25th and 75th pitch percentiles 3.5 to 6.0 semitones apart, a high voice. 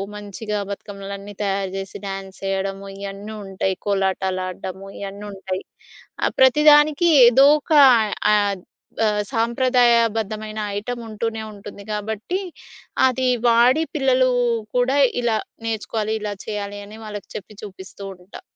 No: average, 3.0 semitones; high, 210 Hz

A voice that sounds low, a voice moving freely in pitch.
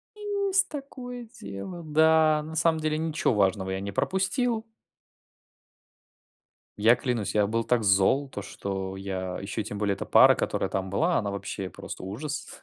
Yes: low, 125 Hz; wide, 8.8 semitones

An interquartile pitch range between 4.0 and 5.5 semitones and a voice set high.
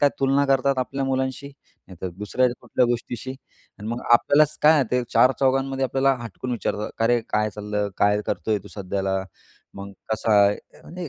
No: average, 4.3 semitones; low, 125 Hz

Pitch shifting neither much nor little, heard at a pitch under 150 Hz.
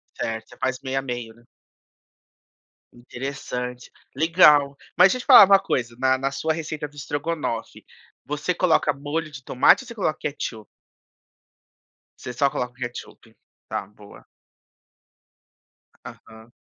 Yes: average, 3.9 semitones; low, 135 Hz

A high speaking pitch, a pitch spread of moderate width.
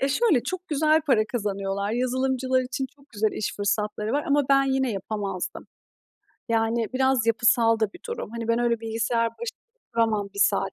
Yes: high, 230 Hz; average, 3.5 semitones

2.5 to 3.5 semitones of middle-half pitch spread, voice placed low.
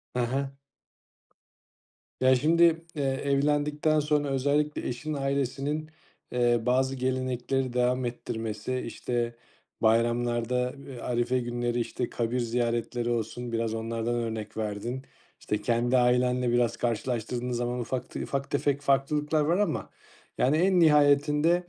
Yes: average, 3.0 semitones; low, 125 Hz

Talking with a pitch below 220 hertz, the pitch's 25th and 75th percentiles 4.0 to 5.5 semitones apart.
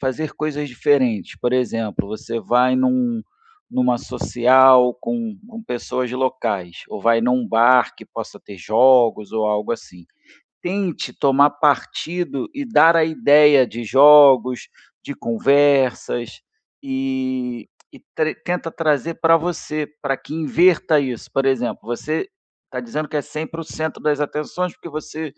Yes: low, 135 Hz; average, 4.3 semitones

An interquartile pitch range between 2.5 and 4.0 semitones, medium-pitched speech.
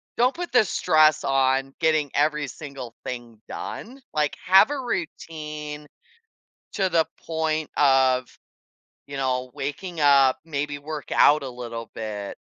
Yes: average, 3.2 semitones; medium, 145 Hz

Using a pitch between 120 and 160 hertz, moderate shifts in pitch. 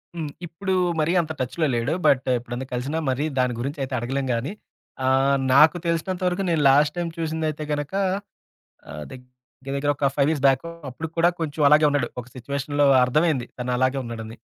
Yes: medium, 140 Hz; average, 3.6 semitones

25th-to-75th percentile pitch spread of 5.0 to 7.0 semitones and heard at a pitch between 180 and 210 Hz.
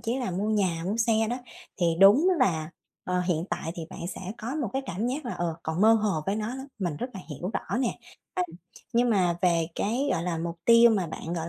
Yes: wide, 5.5 semitones; high, 195 Hz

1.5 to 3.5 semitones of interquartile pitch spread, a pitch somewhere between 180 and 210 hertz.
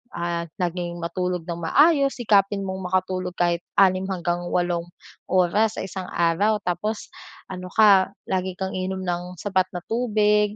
Yes: narrow, 2.5 semitones; medium, 185 Hz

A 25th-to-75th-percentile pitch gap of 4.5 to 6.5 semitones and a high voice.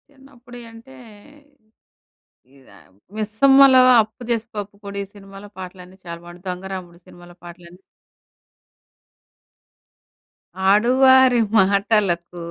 Yes: average, 5.0 semitones; high, 200 Hz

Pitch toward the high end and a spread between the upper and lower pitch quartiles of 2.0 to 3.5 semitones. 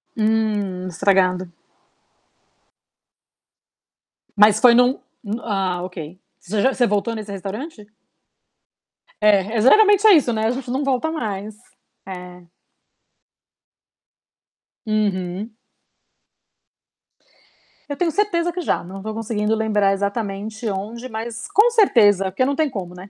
No: high, 215 Hz; average, 4.1 semitones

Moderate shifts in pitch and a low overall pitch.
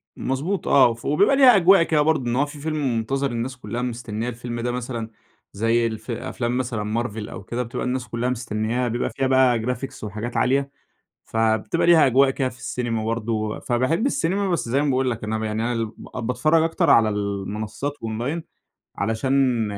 Yes: average, 3.4 semitones; low, 120 Hz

